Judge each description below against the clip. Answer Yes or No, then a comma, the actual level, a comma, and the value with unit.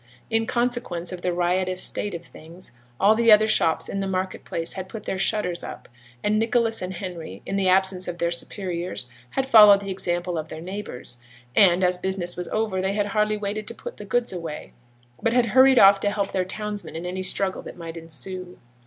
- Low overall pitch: No, high, 190 Hz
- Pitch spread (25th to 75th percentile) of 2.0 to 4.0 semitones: Yes, average, 3.0 semitones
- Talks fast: Yes, fast, 210 wpm